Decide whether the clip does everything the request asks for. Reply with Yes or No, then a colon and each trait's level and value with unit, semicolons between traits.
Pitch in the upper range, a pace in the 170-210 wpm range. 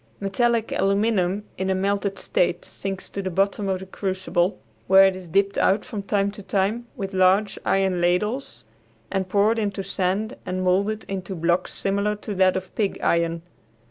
Yes: high, 195 Hz; average, 175 wpm